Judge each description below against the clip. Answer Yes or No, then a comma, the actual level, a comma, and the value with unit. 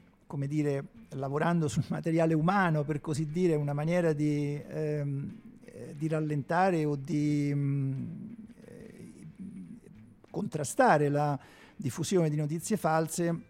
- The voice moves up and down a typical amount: Yes, average, 4.1 semitones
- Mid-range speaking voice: Yes, medium, 160 Hz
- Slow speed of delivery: Yes, slow, 105 wpm